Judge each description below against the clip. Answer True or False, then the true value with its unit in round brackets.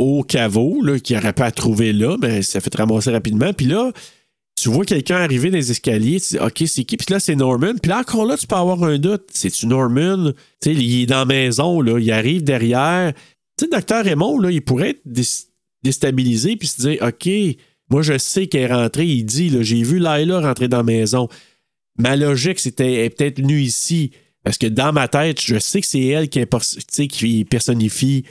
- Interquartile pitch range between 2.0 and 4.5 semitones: False (5.5 semitones)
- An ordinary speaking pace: False (235 wpm)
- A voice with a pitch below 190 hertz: True (135 Hz)